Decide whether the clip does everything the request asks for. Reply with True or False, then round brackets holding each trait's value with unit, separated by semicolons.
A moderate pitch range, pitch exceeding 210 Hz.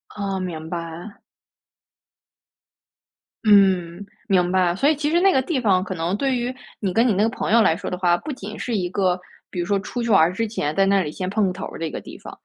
False (4.2 semitones; 195 Hz)